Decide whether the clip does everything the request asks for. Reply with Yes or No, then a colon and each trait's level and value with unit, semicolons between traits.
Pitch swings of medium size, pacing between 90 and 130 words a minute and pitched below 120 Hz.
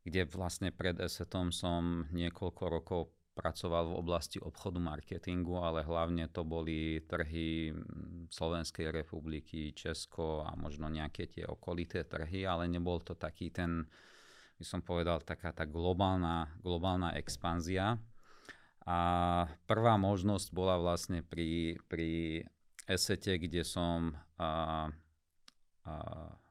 No: narrow, 1.6 semitones; average, 115 wpm; very low, 85 Hz